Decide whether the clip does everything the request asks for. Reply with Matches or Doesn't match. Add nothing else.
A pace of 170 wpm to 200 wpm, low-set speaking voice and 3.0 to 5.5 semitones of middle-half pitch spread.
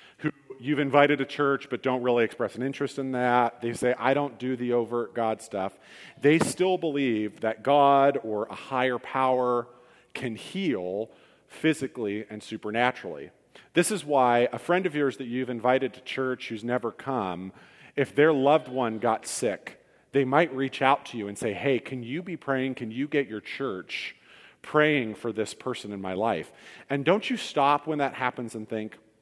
Matches